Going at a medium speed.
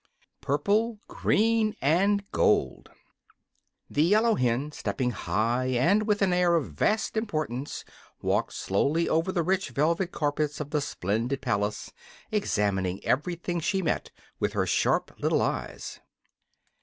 No: slow, 130 wpm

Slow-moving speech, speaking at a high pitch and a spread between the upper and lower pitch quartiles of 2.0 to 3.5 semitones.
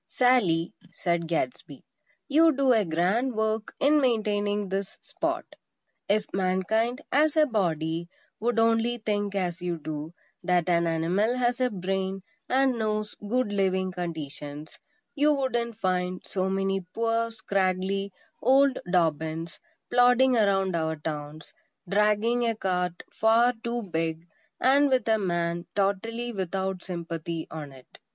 No: slow, 130 wpm; high, 195 Hz; average, 5.2 semitones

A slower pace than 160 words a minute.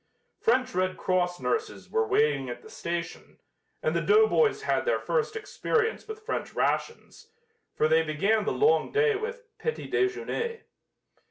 Yes: average, 150 wpm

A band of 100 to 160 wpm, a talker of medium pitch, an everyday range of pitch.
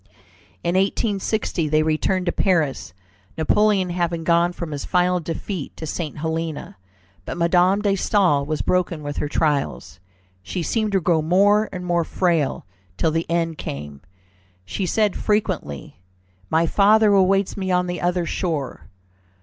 Yes: average, 150 wpm; medium, 175 Hz; average, 3.4 semitones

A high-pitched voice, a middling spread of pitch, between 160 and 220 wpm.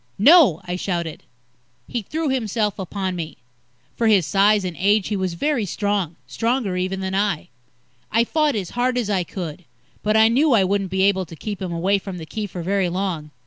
Yes: high, 195 Hz; average, 3.3 semitones; average, 200 wpm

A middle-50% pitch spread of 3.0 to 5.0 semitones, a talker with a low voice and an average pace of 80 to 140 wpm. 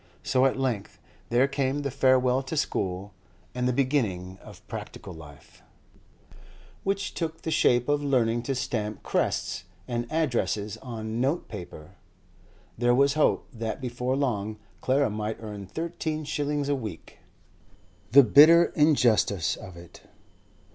Yes: average, 4.7 semitones; low, 125 Hz; slow, 135 wpm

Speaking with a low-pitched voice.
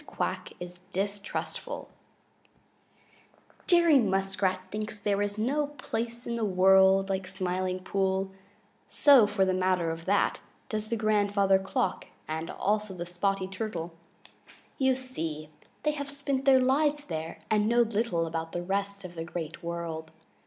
No: high, 195 Hz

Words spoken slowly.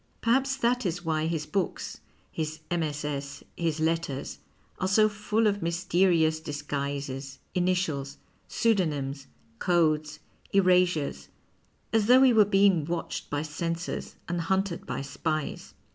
Yes: slow, 125 wpm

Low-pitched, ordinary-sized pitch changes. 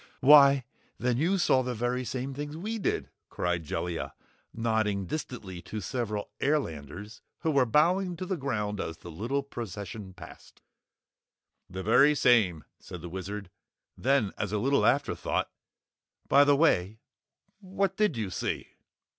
No: low, 120 Hz; wide, 6.2 semitones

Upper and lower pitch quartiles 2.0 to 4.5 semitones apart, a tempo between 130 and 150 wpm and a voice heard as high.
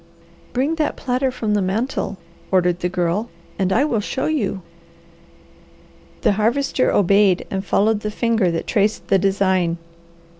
Yes: average, 4.0 semitones; average, 145 wpm; high, 205 Hz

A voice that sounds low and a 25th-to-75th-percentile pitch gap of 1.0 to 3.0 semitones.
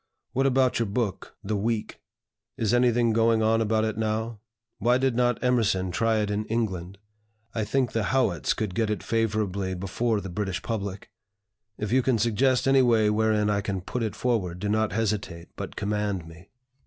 Yes: low, 110 Hz; narrow, 2.6 semitones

